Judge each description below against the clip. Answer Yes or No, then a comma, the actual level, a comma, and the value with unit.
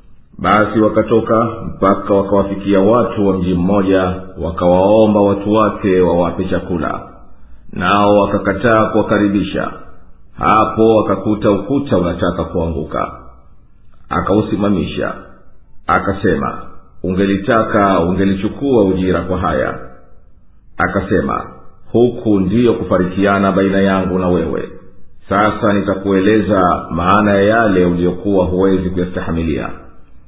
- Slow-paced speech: Yes, slow, 85 wpm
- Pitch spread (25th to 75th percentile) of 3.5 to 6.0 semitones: No, narrow, 2.6 semitones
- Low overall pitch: Yes, very low, 95 Hz